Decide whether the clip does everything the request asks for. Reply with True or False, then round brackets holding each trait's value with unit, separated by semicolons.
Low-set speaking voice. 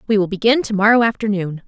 False (210 Hz)